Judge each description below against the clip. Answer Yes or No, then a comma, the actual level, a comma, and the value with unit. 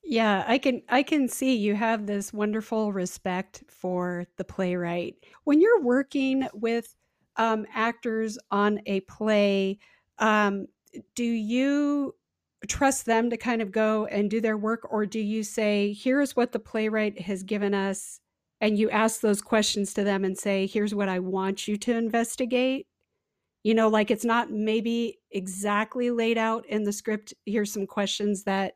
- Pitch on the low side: No, high, 215 Hz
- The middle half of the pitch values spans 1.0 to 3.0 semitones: Yes, narrow, 2.4 semitones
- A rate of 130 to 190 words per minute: Yes, average, 165 wpm